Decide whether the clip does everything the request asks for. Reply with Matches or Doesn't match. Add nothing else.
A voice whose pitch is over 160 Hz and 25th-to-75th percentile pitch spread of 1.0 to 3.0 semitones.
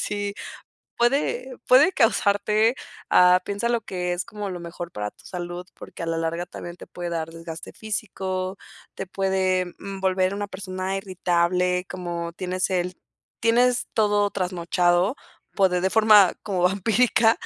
Matches